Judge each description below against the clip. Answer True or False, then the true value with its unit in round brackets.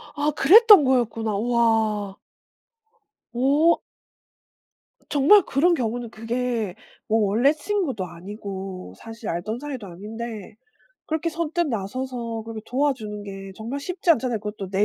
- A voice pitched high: True (230 Hz)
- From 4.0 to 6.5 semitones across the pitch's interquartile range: True (5.2 semitones)